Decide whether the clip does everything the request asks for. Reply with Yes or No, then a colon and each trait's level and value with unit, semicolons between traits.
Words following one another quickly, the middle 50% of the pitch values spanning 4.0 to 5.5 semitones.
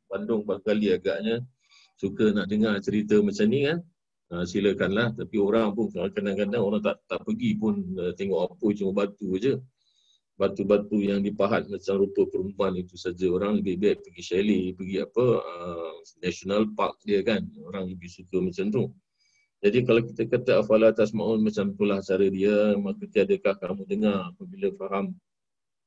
No: fast, 160 wpm; average, 3.1 semitones